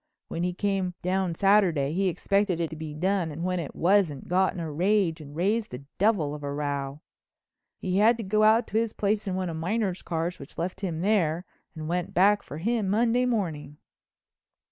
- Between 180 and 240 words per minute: Yes, fast, 205 wpm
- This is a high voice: No, medium, 180 Hz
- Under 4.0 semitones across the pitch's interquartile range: No, average, 4.3 semitones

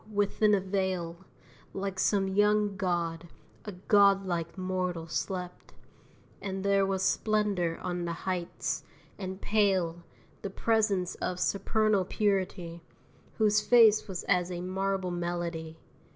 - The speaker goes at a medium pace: No, slow, 120 wpm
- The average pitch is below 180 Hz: No, high, 190 Hz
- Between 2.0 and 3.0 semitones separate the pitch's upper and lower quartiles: Yes, narrow, 2.4 semitones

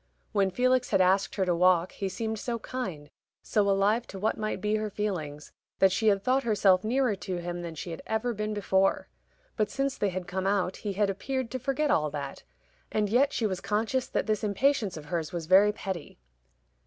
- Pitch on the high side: Yes, high, 200 Hz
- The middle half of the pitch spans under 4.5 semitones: Yes, average, 3.2 semitones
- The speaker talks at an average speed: No, fast, 210 wpm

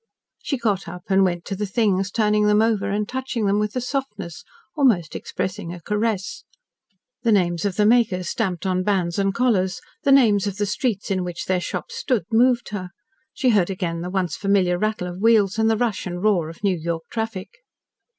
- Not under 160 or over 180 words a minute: No, average, 200 wpm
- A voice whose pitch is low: No, high, 200 Hz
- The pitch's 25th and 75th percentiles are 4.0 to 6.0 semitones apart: No, average, 3.5 semitones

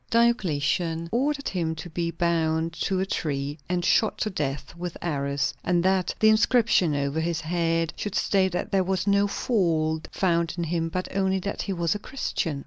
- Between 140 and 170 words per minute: No, average, 185 wpm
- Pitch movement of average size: Yes, average, 3.1 semitones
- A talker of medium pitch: Yes, medium, 170 Hz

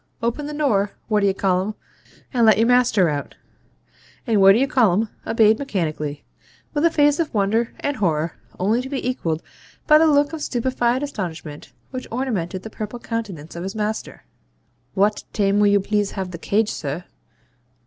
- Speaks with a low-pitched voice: No, high, 215 Hz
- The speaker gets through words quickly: No, average, 170 wpm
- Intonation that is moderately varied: Yes, average, 4.9 semitones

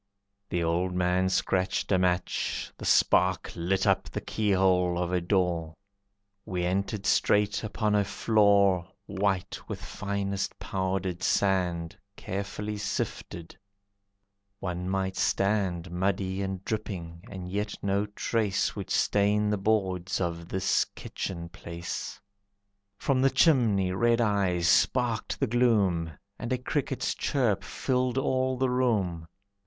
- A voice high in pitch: No, very low, 95 Hz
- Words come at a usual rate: No, slow, 125 wpm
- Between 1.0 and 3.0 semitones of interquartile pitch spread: Yes, average, 2.7 semitones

